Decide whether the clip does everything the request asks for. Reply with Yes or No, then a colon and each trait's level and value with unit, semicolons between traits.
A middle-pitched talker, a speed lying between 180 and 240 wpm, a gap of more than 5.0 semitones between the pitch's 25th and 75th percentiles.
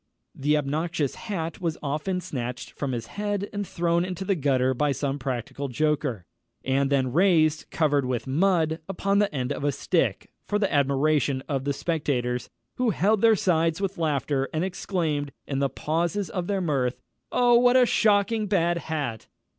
No: medium, 155 Hz; average, 170 wpm; wide, 5.5 semitones